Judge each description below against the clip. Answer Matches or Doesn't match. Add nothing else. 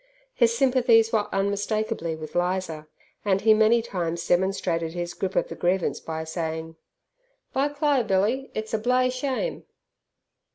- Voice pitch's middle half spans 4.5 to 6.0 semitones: Matches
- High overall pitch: Matches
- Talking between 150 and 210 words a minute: Doesn't match